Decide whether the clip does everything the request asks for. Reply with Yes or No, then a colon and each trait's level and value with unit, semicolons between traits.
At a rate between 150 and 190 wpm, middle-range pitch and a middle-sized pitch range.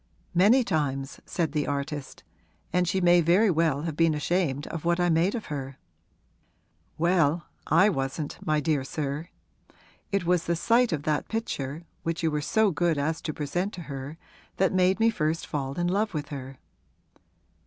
Yes: average, 175 wpm; medium, 165 Hz; average, 3.5 semitones